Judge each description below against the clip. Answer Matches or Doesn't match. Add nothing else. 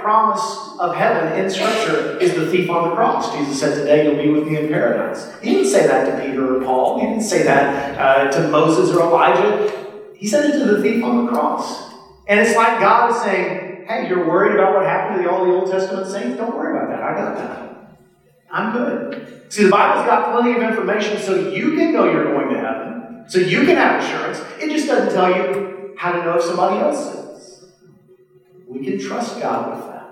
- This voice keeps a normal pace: Doesn't match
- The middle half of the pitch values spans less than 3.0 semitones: Doesn't match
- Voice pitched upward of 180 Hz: Matches